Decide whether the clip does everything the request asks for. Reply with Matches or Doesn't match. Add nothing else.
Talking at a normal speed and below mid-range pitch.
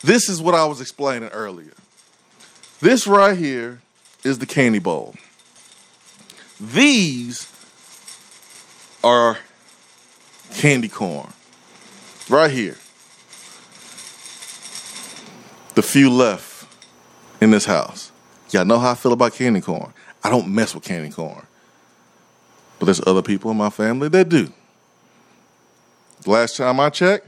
Doesn't match